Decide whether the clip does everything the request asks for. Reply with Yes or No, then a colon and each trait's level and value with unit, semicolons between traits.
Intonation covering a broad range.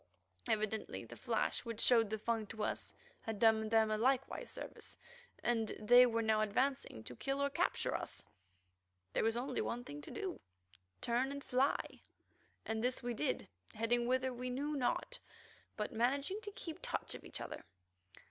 No: average, 3.4 semitones